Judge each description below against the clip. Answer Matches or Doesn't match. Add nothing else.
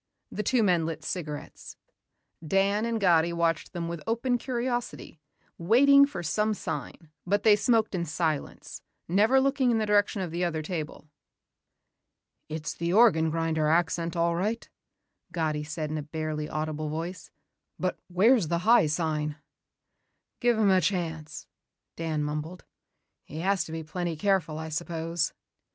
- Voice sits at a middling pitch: Matches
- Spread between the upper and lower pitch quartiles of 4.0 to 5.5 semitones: Matches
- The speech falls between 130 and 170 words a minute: Matches